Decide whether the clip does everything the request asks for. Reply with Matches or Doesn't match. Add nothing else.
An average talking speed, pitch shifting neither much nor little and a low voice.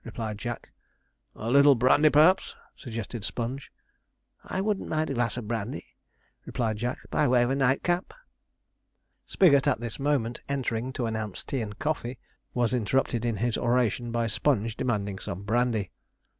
Matches